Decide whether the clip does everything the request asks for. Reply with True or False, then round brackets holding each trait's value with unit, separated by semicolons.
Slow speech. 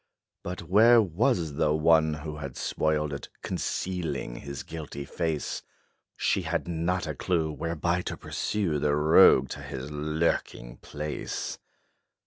True (130 wpm)